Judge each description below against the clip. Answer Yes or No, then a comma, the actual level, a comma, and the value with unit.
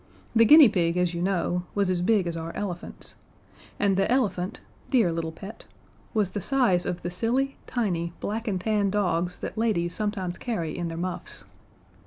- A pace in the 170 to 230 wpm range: Yes, average, 180 wpm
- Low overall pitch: No, medium, 185 Hz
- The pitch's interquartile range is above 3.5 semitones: Yes, average, 3.9 semitones